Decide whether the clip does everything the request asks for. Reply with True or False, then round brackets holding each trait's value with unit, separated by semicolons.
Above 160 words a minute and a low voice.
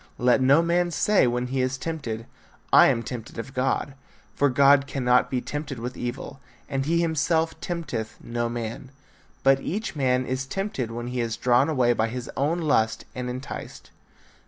True (175 wpm; 130 Hz)